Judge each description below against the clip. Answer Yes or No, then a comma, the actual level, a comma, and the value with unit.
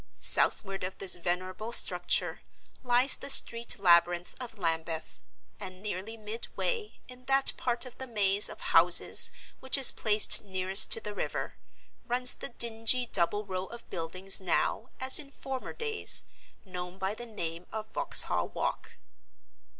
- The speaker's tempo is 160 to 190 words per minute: No, average, 145 wpm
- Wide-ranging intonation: No, average, 4.8 semitones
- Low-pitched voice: No, high, 210 Hz